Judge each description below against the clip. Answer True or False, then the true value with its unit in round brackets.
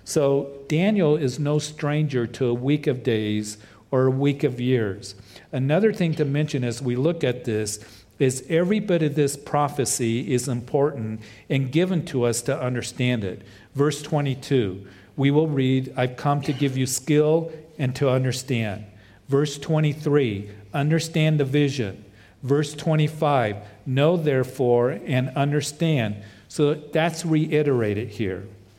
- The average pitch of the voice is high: False (135 Hz)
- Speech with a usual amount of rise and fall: True (4.3 semitones)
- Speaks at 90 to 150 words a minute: True (140 wpm)